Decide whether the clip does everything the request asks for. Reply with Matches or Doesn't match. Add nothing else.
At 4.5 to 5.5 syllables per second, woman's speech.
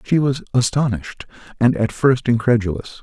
Doesn't match